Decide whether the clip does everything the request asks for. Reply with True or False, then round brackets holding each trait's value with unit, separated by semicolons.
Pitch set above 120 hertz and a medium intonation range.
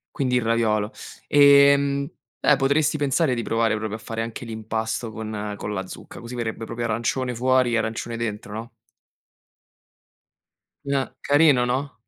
False (115 Hz; 3.5 semitones)